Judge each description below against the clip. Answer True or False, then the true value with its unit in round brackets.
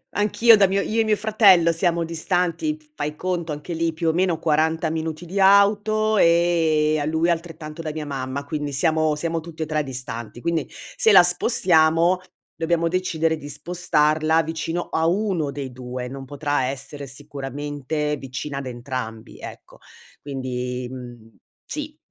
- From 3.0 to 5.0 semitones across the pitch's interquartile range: True (3.5 semitones)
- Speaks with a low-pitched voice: False (160 Hz)